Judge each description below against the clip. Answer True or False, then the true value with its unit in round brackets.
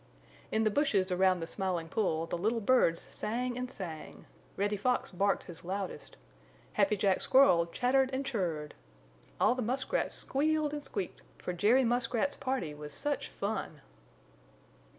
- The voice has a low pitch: False (210 Hz)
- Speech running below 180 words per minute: True (160 wpm)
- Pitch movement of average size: False (6.2 semitones)